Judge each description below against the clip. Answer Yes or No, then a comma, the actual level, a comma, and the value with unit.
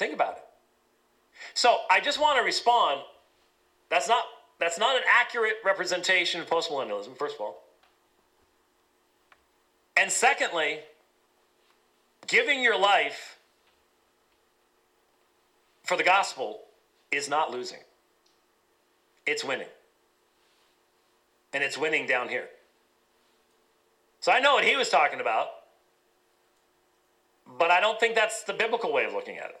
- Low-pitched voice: No, high, 195 Hz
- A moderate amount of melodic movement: No, wide, 6.5 semitones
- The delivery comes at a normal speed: No, slow, 120 wpm